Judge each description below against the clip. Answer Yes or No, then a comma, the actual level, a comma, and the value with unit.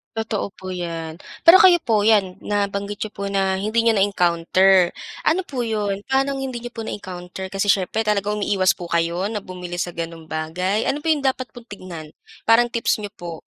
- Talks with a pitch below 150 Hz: No, high, 200 Hz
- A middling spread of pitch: Yes, average, 3.8 semitones